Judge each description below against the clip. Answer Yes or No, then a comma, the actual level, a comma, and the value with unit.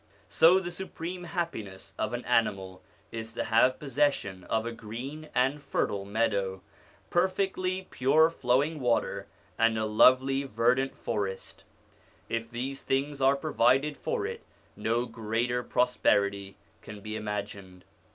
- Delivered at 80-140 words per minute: Yes, slow, 135 wpm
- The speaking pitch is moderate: No, low, 120 Hz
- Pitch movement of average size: Yes, average, 4.7 semitones